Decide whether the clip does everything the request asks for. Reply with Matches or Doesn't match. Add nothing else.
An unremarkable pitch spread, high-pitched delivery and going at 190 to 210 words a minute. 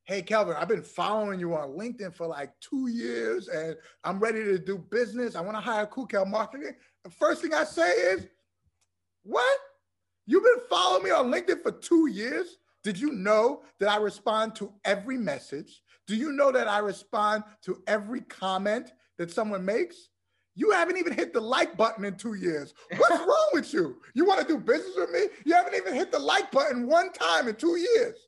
Doesn't match